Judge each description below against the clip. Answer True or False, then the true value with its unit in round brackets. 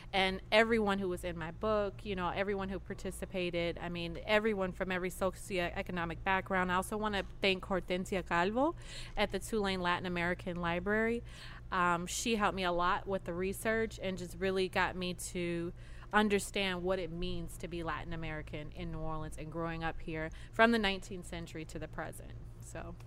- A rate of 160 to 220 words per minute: True (180 wpm)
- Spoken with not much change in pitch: True (2.3 semitones)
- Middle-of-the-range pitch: True (180 Hz)